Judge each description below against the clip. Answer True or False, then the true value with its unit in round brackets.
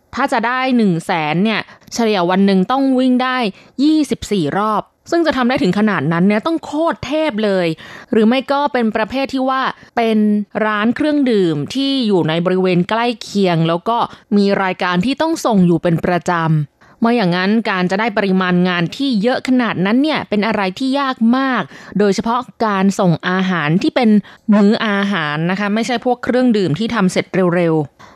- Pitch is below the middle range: False (215 Hz)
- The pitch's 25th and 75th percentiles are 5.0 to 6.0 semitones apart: True (5.4 semitones)